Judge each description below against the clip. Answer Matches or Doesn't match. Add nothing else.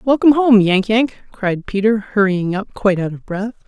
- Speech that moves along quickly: Doesn't match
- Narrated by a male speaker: Doesn't match